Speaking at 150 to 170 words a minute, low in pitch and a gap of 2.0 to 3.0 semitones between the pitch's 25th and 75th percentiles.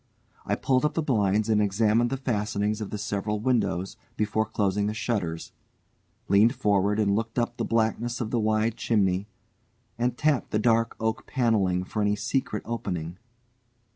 Yes: average, 165 wpm; low, 110 Hz; narrow, 2.4 semitones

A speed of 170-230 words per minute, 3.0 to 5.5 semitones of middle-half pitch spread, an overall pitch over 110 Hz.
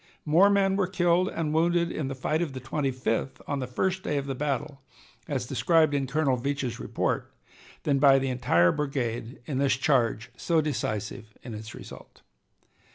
Yes: average, 180 wpm; average, 3.8 semitones; medium, 140 Hz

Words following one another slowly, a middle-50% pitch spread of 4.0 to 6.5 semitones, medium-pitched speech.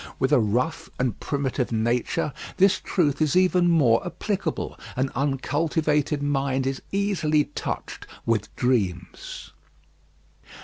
Yes: slow, 115 wpm; average, 4.3 semitones; medium, 145 Hz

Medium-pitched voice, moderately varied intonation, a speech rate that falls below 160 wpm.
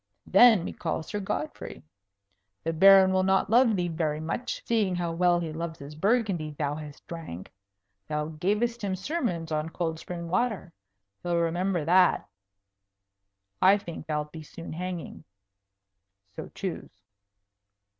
Yes: medium, 175 Hz; average, 3.3 semitones; average, 140 wpm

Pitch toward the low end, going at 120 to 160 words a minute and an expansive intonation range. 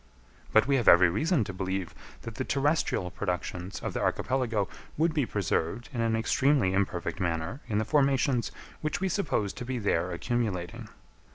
No: low, 110 Hz; average, 170 wpm; wide, 6.4 semitones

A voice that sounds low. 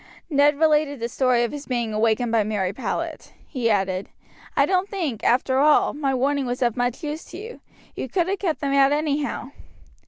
No: very high, 270 Hz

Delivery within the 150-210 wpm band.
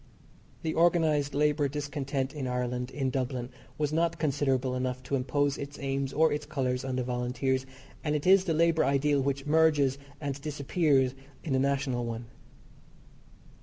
Yes: average, 160 wpm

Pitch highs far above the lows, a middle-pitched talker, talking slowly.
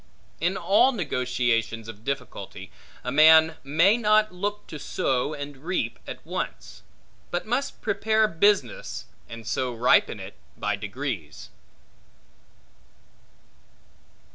Yes: wide, 8.2 semitones; medium, 150 Hz; slow, 110 wpm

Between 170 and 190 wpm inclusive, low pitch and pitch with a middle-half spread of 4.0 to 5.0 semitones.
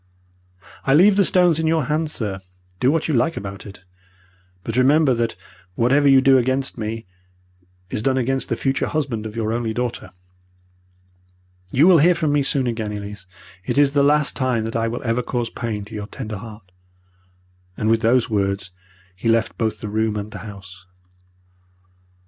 Yes: average, 180 wpm; low, 115 Hz; average, 4.5 semitones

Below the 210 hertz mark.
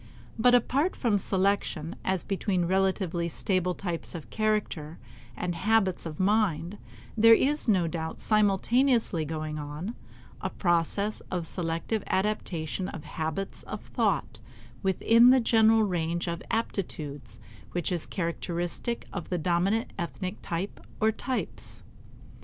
Yes: medium, 185 Hz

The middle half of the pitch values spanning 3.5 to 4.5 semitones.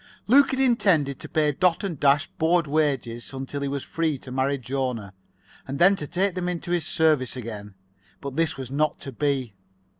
Yes: average, 4.2 semitones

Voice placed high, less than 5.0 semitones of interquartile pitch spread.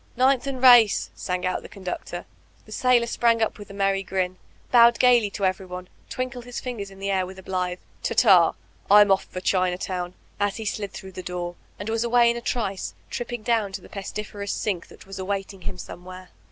Yes: high, 200 Hz; average, 4.1 semitones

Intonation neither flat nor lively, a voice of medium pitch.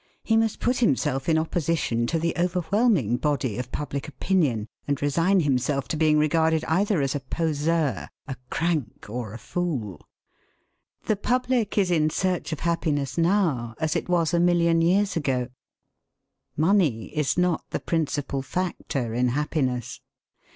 Yes: average, 4.6 semitones; medium, 155 Hz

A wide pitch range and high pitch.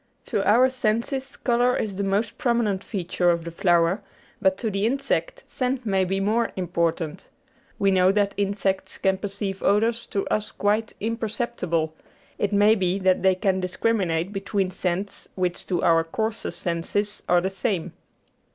No: average, 3.2 semitones; high, 195 Hz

